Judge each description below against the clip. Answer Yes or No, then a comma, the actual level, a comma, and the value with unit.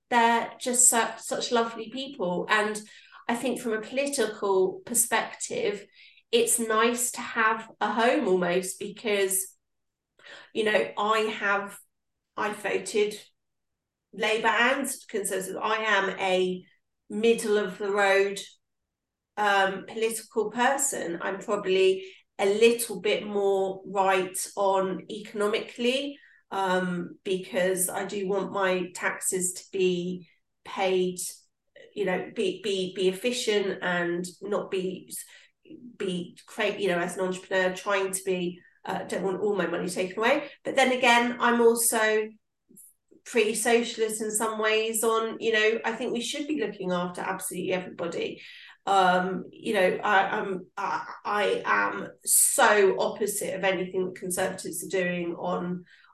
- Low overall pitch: No, high, 205 Hz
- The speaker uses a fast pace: No, slow, 135 wpm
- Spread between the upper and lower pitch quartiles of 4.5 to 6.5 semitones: No, average, 3.6 semitones